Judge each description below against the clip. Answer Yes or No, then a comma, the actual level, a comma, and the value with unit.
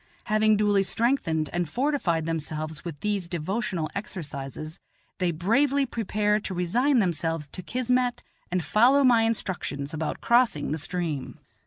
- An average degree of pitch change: No, wide, 6.4 semitones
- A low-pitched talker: No, medium, 185 Hz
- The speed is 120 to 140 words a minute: Yes, slow, 135 wpm